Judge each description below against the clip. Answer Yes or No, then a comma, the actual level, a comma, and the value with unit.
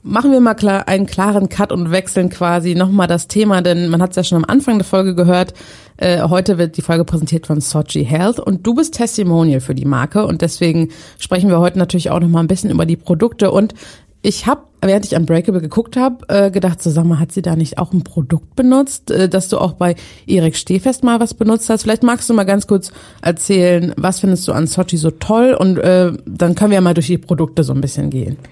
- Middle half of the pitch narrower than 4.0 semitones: Yes, average, 3.3 semitones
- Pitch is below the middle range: No, medium, 180 Hz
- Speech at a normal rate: No, fast, 235 wpm